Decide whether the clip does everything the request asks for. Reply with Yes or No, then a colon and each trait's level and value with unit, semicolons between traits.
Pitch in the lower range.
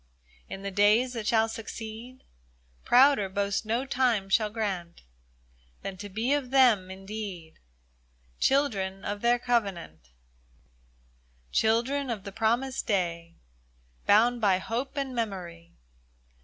No: high, 220 Hz